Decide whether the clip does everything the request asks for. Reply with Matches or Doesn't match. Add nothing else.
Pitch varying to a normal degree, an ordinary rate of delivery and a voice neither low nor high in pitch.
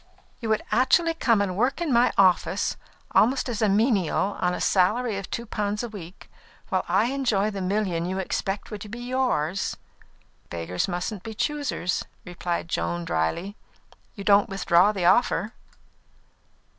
Doesn't match